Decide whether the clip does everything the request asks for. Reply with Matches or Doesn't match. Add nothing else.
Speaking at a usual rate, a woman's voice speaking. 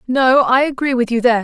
Doesn't match